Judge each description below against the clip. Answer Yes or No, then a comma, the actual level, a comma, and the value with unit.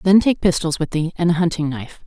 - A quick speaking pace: Yes, fast, 260 wpm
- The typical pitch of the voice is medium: Yes, medium, 165 Hz